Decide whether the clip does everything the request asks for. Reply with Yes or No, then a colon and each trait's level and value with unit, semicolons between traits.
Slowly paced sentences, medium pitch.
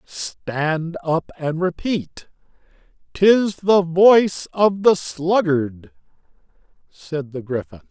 Yes: slow, 100 wpm; medium, 165 Hz